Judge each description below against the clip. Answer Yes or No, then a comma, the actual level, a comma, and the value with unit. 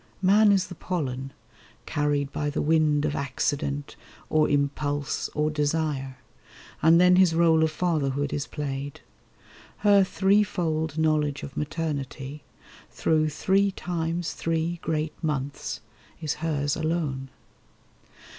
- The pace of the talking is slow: Yes, slow, 115 wpm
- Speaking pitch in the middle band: Yes, medium, 155 Hz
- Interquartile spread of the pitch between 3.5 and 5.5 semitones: No, narrow, 2.6 semitones